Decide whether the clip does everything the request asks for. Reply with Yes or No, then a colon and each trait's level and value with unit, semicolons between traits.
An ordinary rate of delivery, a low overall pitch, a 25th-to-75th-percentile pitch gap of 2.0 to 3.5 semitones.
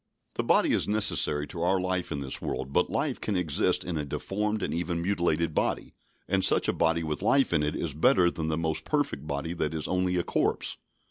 No: fast, 220 wpm; very low, 85 Hz; average, 3.2 semitones